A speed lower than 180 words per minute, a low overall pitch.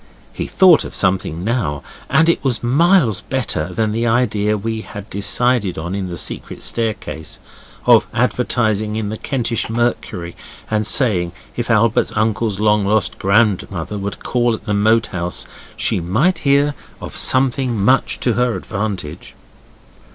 Yes: average, 150 wpm; low, 110 Hz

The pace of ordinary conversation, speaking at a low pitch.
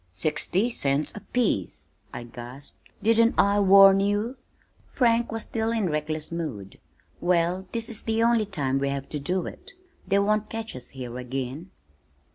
No: average, 155 wpm; medium, 185 Hz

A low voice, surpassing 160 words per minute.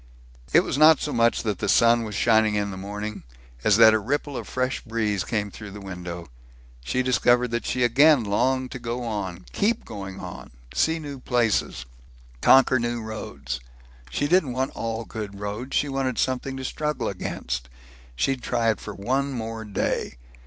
Yes: low, 115 Hz; average, 180 wpm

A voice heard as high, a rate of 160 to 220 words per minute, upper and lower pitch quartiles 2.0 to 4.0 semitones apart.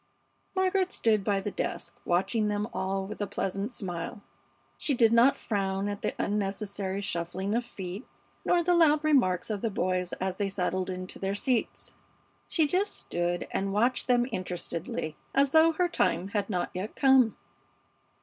No: high, 205 Hz; average, 165 wpm; average, 4.6 semitones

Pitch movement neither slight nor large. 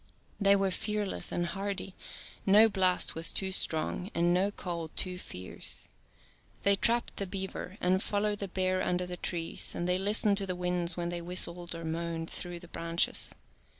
No: narrow, 2.3 semitones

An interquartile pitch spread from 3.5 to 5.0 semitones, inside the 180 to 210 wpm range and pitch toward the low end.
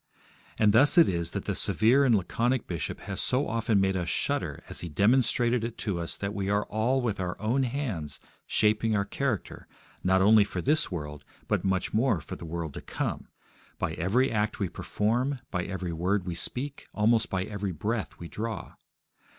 Yes: average, 4.4 semitones; average, 190 wpm; low, 105 Hz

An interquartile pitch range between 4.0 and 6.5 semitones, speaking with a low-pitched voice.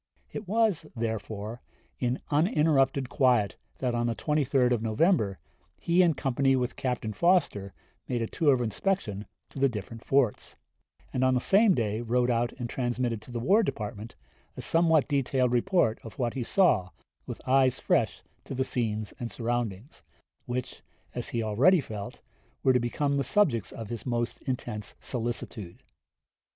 No: average, 3.6 semitones; low, 125 Hz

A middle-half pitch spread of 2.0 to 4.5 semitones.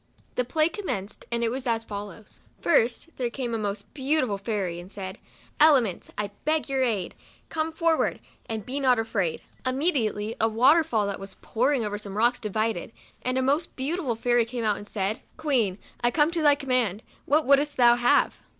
No: average, 5.0 semitones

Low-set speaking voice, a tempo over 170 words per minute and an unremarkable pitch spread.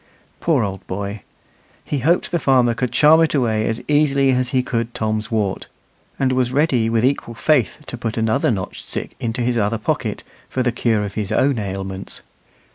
Yes: low, 120 Hz; average, 190 wpm; average, 3.5 semitones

